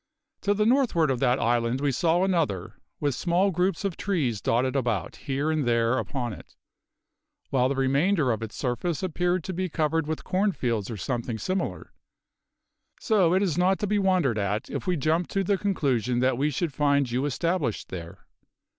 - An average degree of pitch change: No, wide, 6.7 semitones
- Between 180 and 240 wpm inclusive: Yes, average, 185 wpm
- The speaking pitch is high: No, medium, 145 Hz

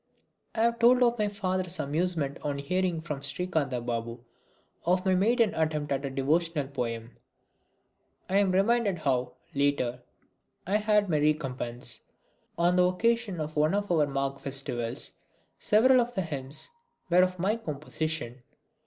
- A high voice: No, medium, 160 Hz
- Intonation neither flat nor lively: No, wide, 5.9 semitones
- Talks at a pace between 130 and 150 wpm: Yes, average, 145 wpm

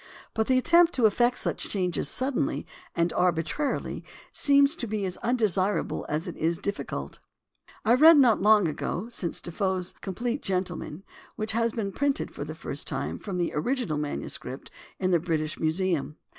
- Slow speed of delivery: No, average, 155 wpm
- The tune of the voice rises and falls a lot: Yes, wide, 5.9 semitones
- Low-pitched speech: No, high, 195 Hz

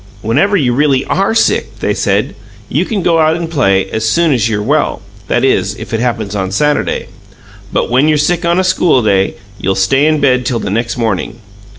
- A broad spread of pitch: Yes, wide, 6.2 semitones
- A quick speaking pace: Yes, fast, 210 wpm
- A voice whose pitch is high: No, low, 130 Hz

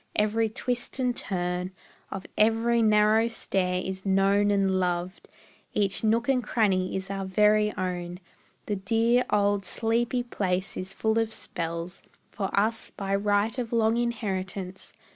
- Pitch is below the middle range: No, high, 205 Hz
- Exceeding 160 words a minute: No, average, 145 wpm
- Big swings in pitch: No, average, 3.1 semitones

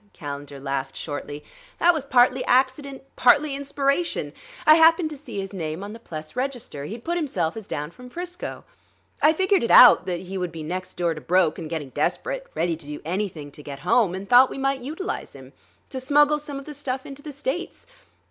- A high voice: Yes, high, 245 Hz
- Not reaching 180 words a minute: No, fast, 205 wpm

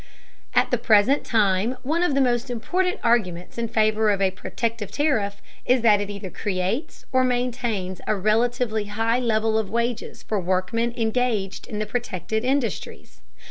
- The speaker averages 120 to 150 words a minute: No, average, 160 wpm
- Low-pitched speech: No, high, 225 Hz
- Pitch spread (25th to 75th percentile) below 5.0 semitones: Yes, average, 3.2 semitones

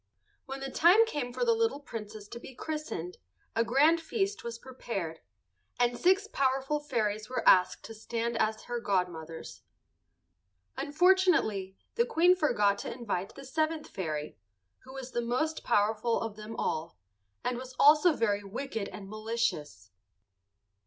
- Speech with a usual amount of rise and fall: No, wide, 6.3 semitones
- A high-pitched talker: Yes, high, 240 Hz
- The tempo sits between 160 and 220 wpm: No, average, 145 wpm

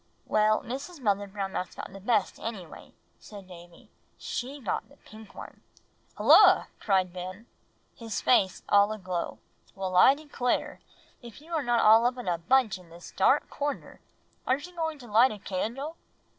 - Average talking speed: Yes, average, 175 wpm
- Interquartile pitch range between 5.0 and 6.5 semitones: Yes, average, 5.3 semitones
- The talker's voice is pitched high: Yes, high, 215 Hz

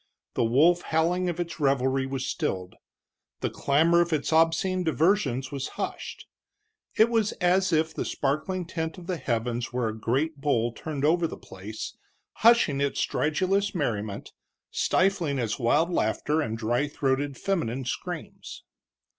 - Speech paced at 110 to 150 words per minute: Yes, average, 145 wpm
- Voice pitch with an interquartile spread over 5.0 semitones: Yes, wide, 5.5 semitones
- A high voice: No, medium, 150 Hz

